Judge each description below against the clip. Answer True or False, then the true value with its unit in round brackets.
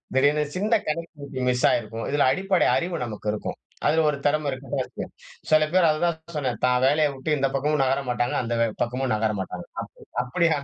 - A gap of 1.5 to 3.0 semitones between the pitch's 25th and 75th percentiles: False (3.6 semitones)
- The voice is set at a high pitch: False (140 Hz)